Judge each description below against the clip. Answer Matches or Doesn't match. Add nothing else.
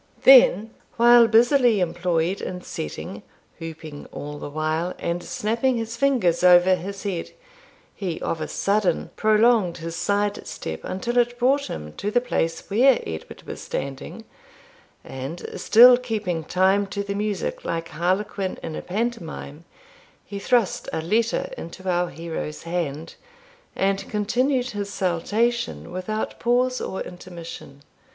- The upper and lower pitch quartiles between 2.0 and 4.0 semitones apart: Doesn't match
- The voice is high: Matches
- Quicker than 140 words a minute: Doesn't match